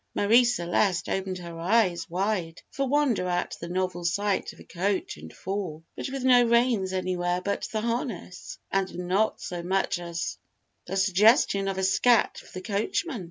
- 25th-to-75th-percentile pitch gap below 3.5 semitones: No, average, 3.8 semitones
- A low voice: No, high, 190 Hz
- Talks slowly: No, average, 170 wpm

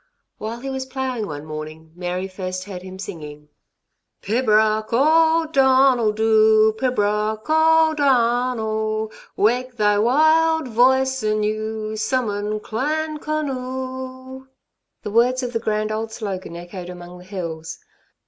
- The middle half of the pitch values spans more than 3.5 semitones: Yes, average, 4.2 semitones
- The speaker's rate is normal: No, slow, 120 wpm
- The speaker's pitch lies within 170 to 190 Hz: No, high, 220 Hz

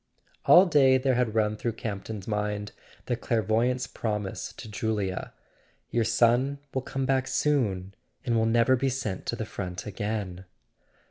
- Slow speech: No, average, 155 wpm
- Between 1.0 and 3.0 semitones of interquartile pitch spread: No, average, 3.5 semitones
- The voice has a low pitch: Yes, low, 115 Hz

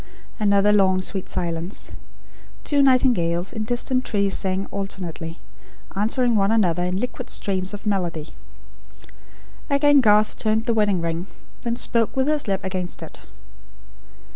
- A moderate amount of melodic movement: Yes, average, 4.0 semitones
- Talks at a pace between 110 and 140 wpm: Yes, slow, 135 wpm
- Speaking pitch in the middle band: No, high, 200 Hz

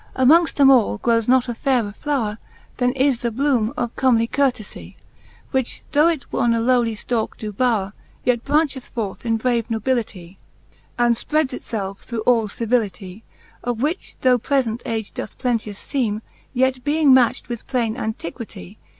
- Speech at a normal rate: Yes, average, 165 wpm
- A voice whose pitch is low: No, high, 240 Hz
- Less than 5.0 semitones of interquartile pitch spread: Yes, average, 2.9 semitones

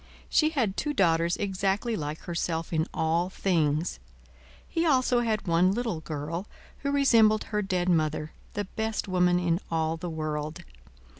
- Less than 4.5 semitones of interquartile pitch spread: No, average, 5.0 semitones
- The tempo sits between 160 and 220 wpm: No, average, 150 wpm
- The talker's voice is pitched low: No, medium, 180 Hz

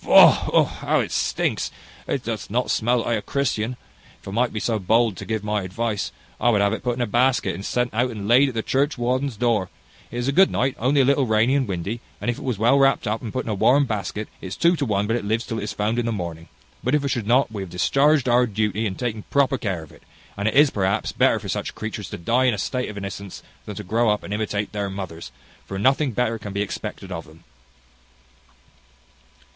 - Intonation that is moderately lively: Yes, average, 3.7 semitones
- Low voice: Yes, low, 110 Hz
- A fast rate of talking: Yes, fast, 250 wpm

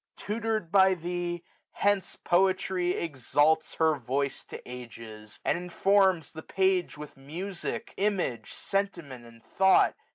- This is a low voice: No, medium, 175 Hz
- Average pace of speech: No, slow, 120 wpm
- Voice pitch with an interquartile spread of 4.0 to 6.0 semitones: Yes, average, 5.2 semitones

